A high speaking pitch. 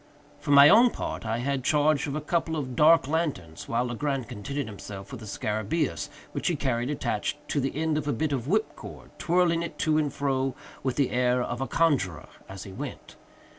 No: medium, 140 Hz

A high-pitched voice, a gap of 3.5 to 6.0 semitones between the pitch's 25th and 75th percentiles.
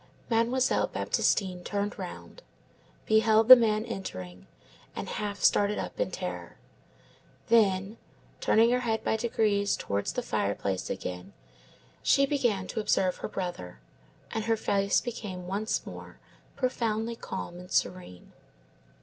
Yes: high, 210 Hz; average, 3.8 semitones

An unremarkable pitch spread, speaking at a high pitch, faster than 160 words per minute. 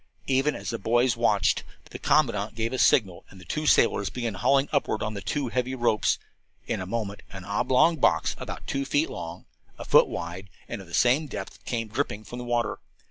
No: average, 4.4 semitones; low, 115 Hz; average, 200 wpm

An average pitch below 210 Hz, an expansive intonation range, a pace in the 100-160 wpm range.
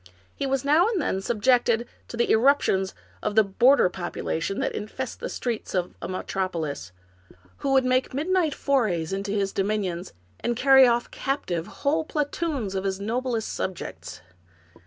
No: high, 230 Hz; wide, 5.9 semitones; average, 155 wpm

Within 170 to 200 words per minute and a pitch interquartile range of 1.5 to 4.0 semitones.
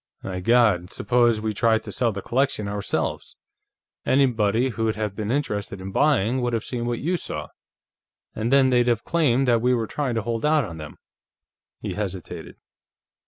Yes: average, 175 wpm; average, 3.4 semitones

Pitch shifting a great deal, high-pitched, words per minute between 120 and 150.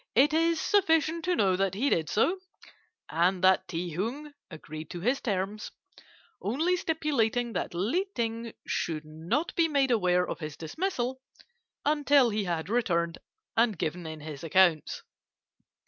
Yes: wide, 8.6 semitones; high, 215 Hz; average, 145 wpm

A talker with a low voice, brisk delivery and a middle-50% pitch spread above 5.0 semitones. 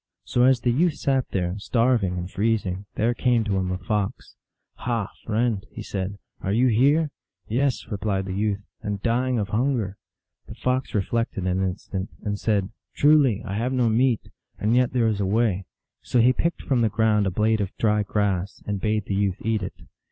No: low, 110 Hz; fast, 210 wpm; average, 3.7 semitones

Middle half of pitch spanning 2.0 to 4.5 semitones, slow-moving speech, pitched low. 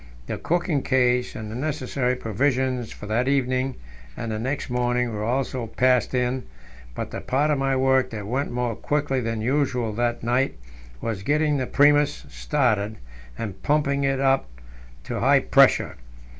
No: average, 2.7 semitones; average, 160 wpm; low, 130 Hz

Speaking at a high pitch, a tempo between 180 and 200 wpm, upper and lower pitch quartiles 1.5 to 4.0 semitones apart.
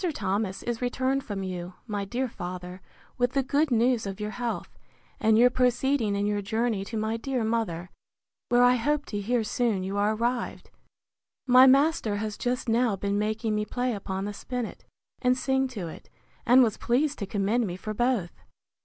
Yes: high, 225 Hz; average, 185 wpm; average, 3.5 semitones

